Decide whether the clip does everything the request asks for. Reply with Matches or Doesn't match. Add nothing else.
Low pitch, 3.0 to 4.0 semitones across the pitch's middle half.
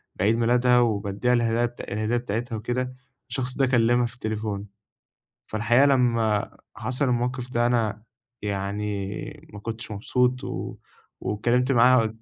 Doesn't match